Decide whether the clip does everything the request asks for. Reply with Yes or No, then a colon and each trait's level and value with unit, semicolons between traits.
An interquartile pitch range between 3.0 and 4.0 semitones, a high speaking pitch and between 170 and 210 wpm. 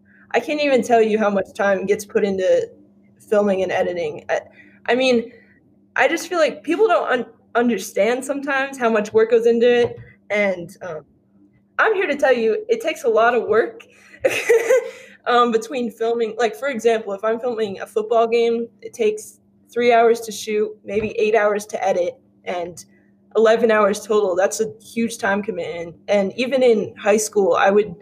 Yes: average, 3.4 semitones; high, 230 Hz; average, 180 wpm